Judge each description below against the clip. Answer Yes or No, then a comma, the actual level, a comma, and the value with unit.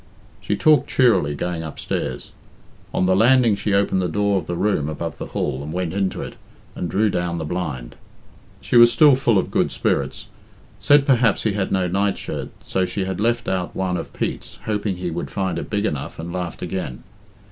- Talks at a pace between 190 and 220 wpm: Yes, average, 200 wpm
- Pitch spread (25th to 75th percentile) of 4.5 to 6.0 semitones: No, average, 3.5 semitones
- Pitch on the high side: No, very low, 95 Hz